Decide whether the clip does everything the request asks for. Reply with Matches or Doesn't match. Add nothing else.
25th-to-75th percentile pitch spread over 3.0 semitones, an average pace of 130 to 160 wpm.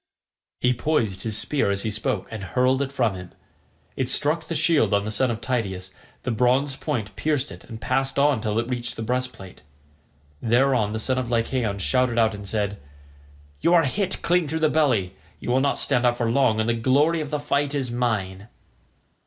Doesn't match